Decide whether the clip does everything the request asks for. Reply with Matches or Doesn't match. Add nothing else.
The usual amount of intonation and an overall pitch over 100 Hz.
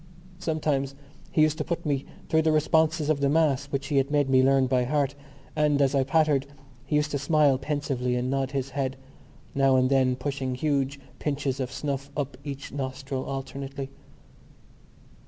Doesn't match